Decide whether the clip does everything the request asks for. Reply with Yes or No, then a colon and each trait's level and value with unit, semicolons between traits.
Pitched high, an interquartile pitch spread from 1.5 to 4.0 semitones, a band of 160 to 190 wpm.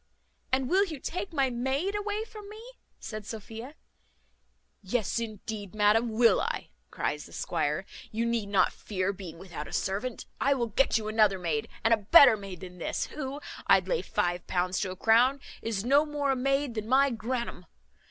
No: high, 230 Hz; average, 5.3 semitones; average, 180 wpm